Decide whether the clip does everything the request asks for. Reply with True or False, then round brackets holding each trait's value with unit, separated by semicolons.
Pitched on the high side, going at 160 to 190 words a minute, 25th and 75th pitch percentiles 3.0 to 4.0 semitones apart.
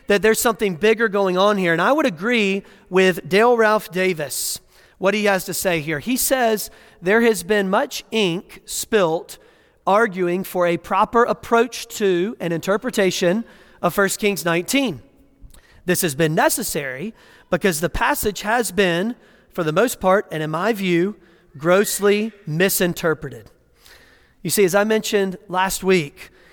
False (200 Hz; 150 wpm; 3.5 semitones)